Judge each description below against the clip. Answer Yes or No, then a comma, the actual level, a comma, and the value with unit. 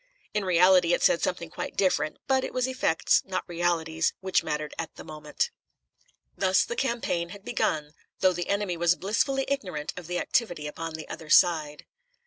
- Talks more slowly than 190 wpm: Yes, average, 175 wpm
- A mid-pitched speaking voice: Yes, medium, 175 Hz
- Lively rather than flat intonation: No, average, 3.8 semitones